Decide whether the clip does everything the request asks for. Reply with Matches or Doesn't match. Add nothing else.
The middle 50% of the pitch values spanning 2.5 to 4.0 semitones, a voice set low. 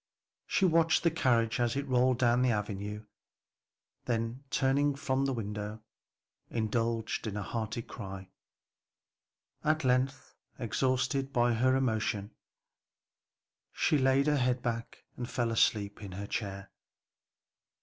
Matches